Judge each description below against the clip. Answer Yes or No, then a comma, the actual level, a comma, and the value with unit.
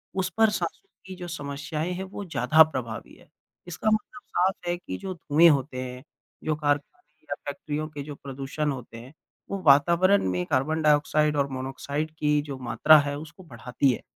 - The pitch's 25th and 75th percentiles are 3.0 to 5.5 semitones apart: Yes, average, 3.9 semitones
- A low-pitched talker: No, medium, 150 Hz